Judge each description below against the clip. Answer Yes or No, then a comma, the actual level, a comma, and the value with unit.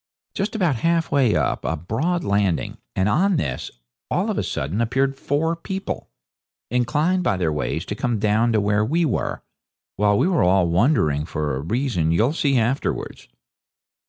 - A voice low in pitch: Yes, low, 115 Hz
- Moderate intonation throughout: No, wide, 8.4 semitones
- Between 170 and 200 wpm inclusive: Yes, average, 175 wpm